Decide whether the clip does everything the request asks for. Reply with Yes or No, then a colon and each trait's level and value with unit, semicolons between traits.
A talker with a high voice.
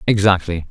No: very low, 95 Hz